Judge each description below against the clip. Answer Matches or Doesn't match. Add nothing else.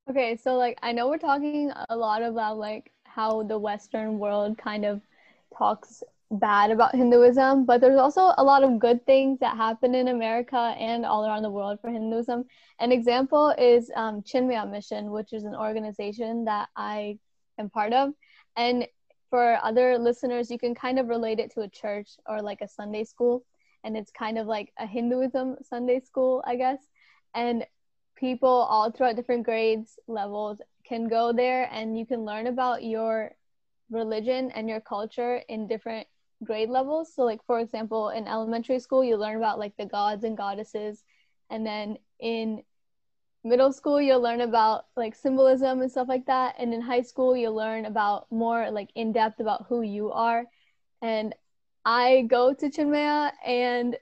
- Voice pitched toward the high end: Matches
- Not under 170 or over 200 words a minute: Matches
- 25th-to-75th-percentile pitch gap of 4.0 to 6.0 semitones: Doesn't match